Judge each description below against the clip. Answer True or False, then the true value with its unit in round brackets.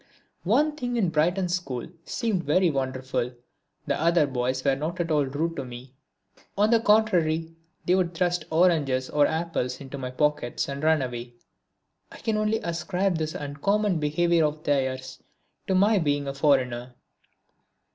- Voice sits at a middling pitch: True (155 Hz)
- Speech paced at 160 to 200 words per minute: True (165 wpm)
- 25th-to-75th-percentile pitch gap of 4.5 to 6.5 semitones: True (4.9 semitones)